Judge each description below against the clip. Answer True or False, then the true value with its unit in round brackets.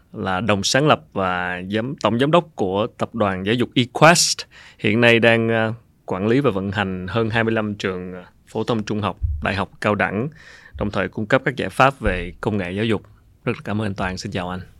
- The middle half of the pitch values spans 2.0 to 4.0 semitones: True (3.3 semitones)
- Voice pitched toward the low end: True (105 Hz)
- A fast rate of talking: False (220 wpm)